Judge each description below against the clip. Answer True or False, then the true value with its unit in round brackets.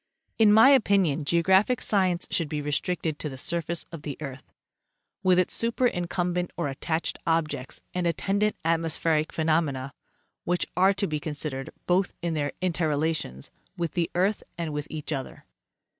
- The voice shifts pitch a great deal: False (3.2 semitones)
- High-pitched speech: False (165 Hz)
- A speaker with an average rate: True (155 wpm)